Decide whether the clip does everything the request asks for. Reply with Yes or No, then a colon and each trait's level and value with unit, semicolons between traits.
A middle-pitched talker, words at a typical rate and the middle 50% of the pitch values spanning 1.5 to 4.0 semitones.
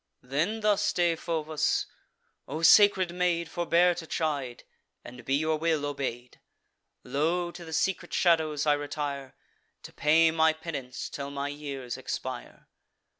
No: medium, 155 Hz; slow, 130 wpm; average, 3.2 semitones